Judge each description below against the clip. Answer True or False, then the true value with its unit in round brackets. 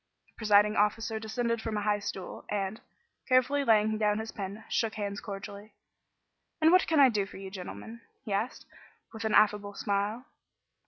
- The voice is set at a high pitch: True (215 Hz)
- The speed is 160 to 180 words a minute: True (170 wpm)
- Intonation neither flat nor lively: False (1.8 semitones)